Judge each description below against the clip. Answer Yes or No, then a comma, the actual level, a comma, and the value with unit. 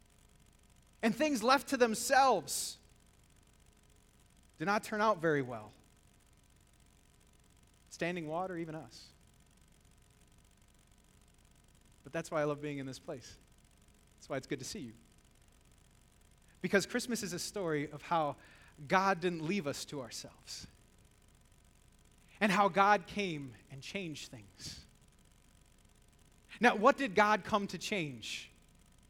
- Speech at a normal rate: No, slow, 120 wpm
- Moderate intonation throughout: No, wide, 6.5 semitones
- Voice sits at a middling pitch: Yes, medium, 175 Hz